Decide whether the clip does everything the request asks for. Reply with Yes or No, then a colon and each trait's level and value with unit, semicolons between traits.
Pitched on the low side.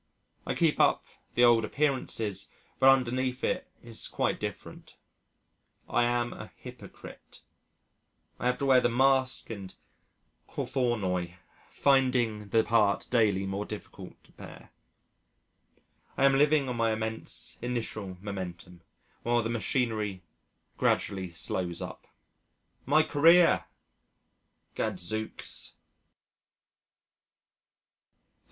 Yes: low, 115 Hz